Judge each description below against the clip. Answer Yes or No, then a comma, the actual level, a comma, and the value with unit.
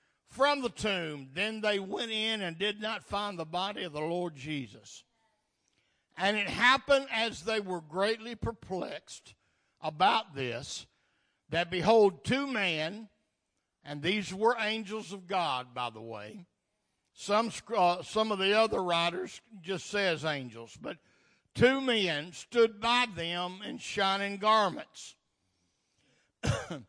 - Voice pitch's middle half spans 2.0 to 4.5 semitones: No, average, 5.0 semitones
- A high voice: Yes, high, 195 Hz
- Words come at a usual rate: No, slow, 130 wpm